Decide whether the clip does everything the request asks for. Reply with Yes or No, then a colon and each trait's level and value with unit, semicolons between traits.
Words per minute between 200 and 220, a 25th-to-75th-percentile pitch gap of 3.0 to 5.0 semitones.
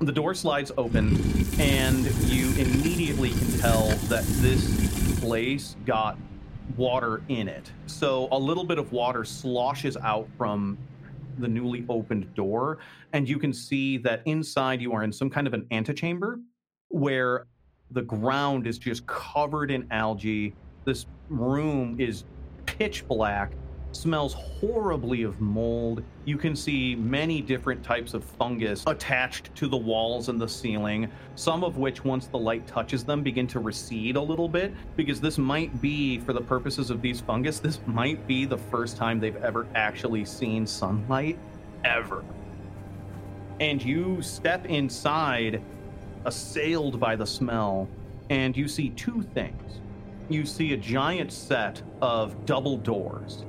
No: average, 150 wpm; average, 4.4 semitones